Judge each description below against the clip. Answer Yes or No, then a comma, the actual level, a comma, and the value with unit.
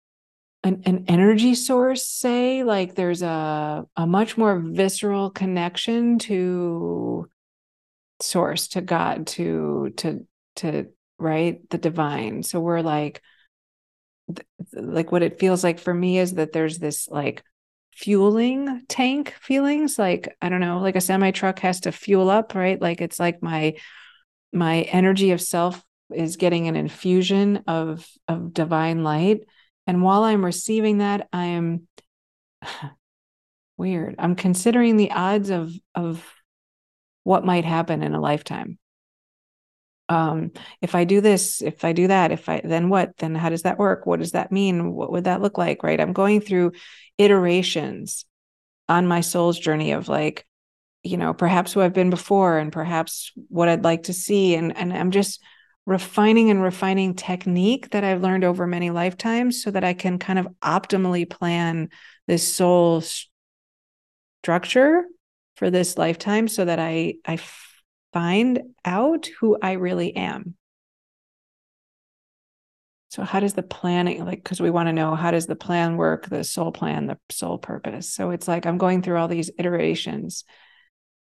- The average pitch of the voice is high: No, medium, 180 Hz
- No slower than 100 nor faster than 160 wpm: Yes, average, 155 wpm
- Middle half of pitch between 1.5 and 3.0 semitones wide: Yes, average, 2.7 semitones